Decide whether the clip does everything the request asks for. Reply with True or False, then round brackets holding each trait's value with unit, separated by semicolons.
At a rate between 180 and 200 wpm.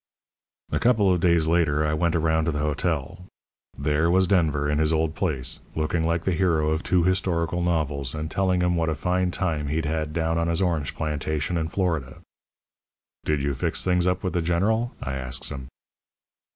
True (190 wpm)